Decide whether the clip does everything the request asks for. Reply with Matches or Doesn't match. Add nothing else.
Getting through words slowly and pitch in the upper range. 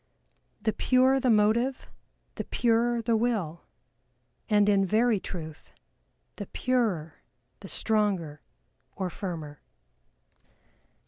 Matches